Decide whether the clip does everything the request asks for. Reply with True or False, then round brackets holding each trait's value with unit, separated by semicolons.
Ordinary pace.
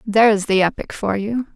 True (195 wpm)